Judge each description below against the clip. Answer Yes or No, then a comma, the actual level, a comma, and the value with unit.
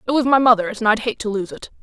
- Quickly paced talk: Yes, fast, 330 wpm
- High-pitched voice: Yes, high, 230 Hz